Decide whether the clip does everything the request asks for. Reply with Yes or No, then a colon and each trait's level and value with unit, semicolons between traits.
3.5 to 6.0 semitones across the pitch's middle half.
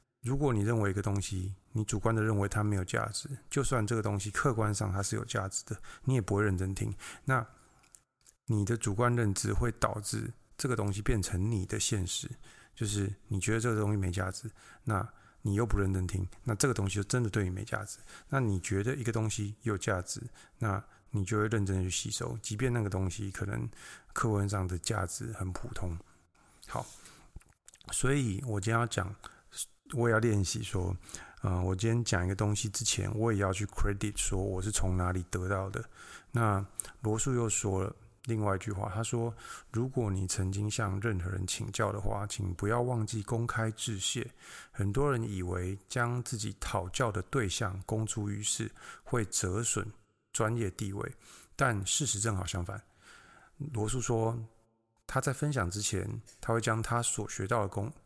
No: average, 2.8 semitones